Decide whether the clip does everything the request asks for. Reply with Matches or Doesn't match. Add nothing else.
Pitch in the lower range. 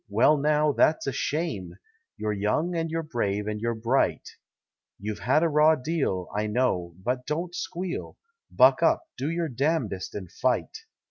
Matches